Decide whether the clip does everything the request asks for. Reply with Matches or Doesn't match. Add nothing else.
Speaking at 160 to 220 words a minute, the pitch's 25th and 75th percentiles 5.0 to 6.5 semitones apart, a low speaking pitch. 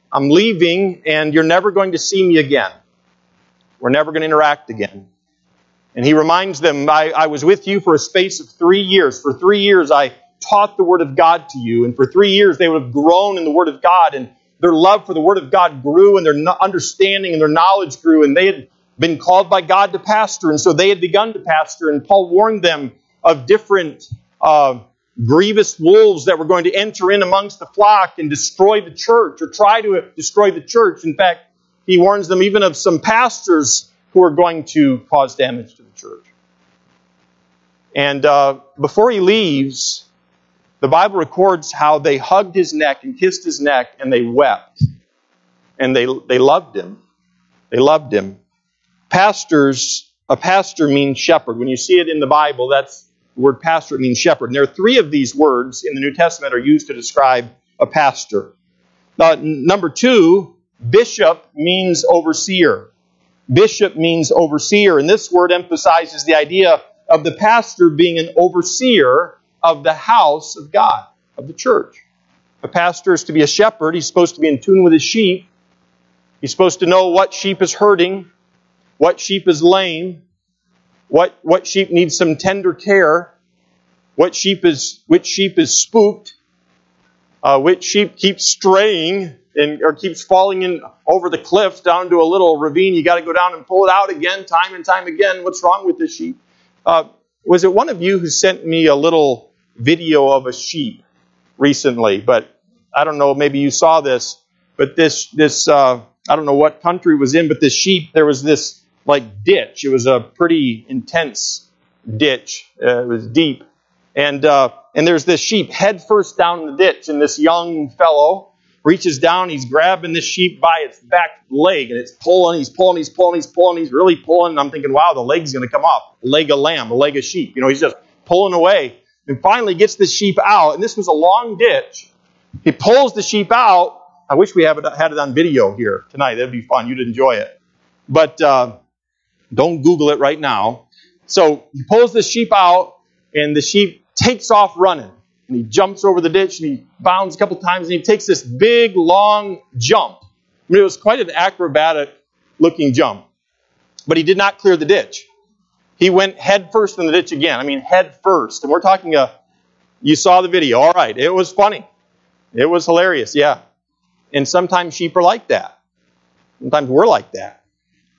Doesn't match